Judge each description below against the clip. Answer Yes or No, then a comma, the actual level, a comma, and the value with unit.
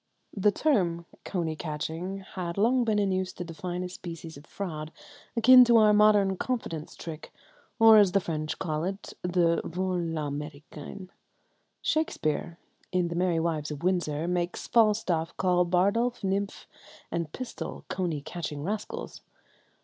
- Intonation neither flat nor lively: Yes, average, 3.7 semitones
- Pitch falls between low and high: Yes, medium, 180 Hz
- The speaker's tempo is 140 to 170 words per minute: Yes, average, 145 wpm